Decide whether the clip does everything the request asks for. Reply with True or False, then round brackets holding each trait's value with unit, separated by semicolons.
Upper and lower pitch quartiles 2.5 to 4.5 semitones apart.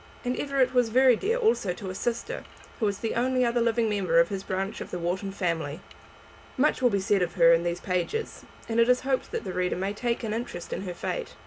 False (5.3 semitones)